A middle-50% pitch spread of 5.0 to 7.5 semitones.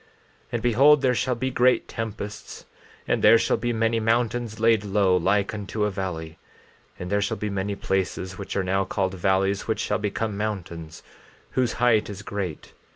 No: average, 2.8 semitones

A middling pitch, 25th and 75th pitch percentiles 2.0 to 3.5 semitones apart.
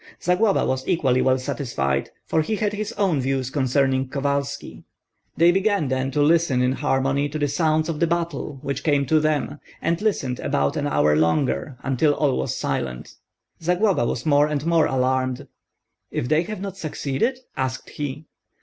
No: medium, 145 Hz; average, 4.0 semitones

